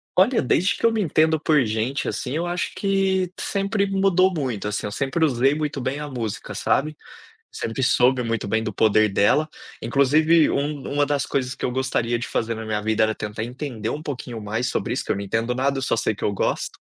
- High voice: No, low, 130 Hz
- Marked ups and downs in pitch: Yes, wide, 5.7 semitones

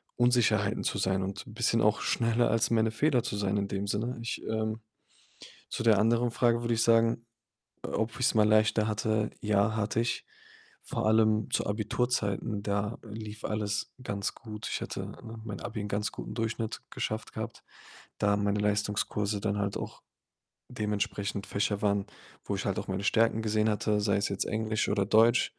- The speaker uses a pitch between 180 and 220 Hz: No, low, 110 Hz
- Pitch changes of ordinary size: No, narrow, 1.8 semitones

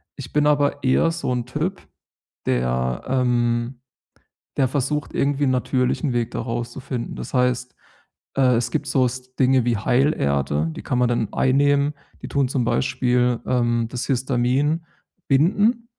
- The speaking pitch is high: No, low, 125 Hz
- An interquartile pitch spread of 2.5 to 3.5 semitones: Yes, average, 2.8 semitones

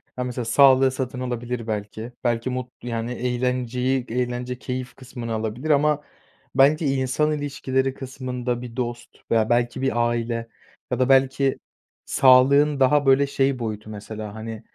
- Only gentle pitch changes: Yes, narrow, 2.2 semitones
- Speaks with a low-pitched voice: Yes, low, 125 Hz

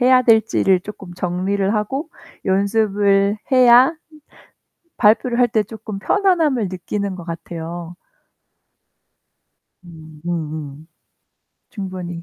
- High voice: Yes, high, 200 Hz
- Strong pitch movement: No, average, 4.4 semitones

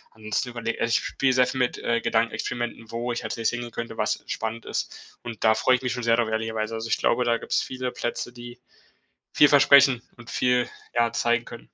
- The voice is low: Yes, low, 120 Hz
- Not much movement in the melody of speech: Yes, narrow, 1.4 semitones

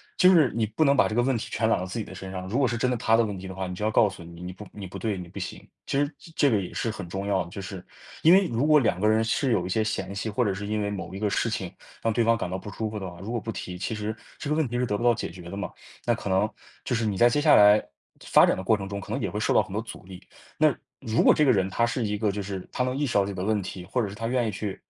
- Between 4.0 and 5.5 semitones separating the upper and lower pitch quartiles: No, average, 3.5 semitones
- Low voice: Yes, low, 105 Hz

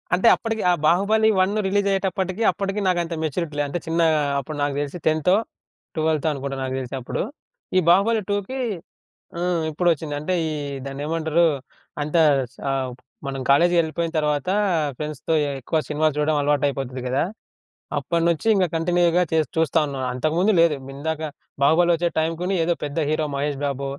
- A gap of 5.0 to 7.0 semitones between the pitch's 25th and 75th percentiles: No, average, 3.3 semitones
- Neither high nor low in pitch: Yes, medium, 160 Hz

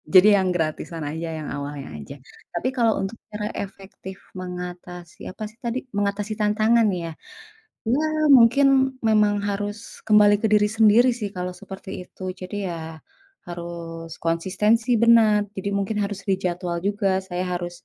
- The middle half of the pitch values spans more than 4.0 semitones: No, average, 3.2 semitones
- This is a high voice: Yes, high, 195 Hz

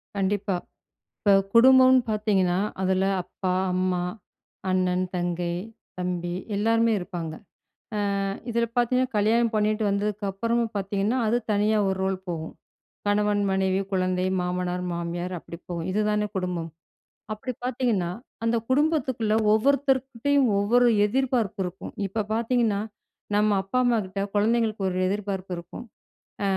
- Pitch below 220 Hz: Yes, high, 205 Hz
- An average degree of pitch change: Yes, average, 3.9 semitones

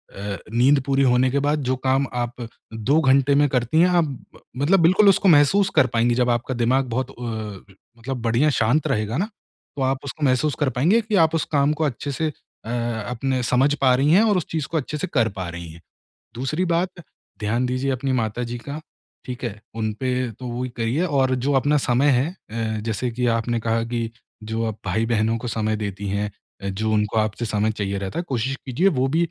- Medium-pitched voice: No, low, 125 Hz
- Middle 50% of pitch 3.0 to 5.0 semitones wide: Yes, average, 4.0 semitones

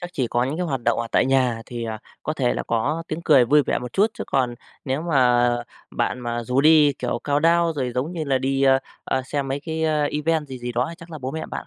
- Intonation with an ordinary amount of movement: Yes, average, 4.0 semitones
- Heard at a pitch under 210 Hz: Yes, low, 135 Hz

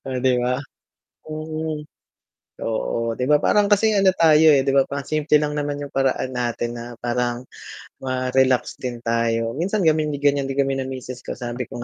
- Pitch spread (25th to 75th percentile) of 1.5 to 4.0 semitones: Yes, average, 3.7 semitones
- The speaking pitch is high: No, low, 135 Hz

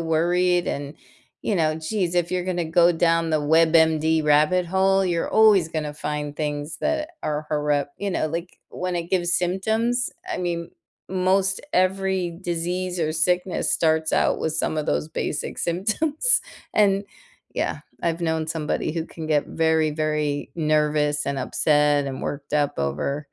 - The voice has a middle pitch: Yes, medium, 165 Hz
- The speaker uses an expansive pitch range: No, average, 3.1 semitones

